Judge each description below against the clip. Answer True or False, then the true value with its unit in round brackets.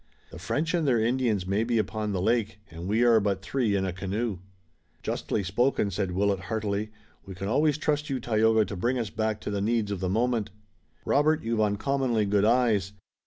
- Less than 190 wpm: False (200 wpm)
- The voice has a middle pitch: False (110 Hz)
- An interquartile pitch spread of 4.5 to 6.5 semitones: False (3.4 semitones)